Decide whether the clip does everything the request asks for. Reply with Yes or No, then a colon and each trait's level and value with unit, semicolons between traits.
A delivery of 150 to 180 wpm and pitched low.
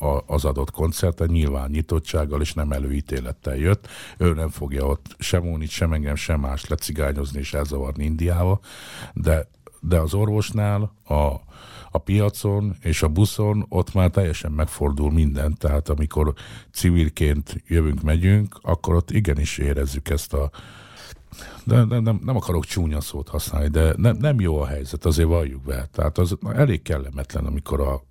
Yes: fast, 155 wpm; very low, 80 Hz